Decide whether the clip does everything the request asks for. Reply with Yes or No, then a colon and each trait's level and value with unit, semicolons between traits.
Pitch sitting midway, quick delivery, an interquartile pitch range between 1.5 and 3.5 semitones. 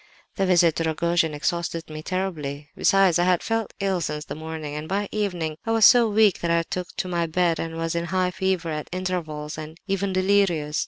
Yes: medium, 170 Hz; fast, 210 wpm; average, 3.1 semitones